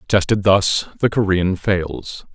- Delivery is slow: Yes, slow, 130 wpm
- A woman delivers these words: No, male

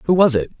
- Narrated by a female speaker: No, male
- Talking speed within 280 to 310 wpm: Yes, fast, 300 wpm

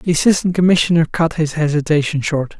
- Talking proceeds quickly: No, average, 160 wpm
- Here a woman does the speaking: No, male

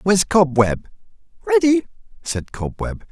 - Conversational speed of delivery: No, slow, 95 wpm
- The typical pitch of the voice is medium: Yes, medium, 150 Hz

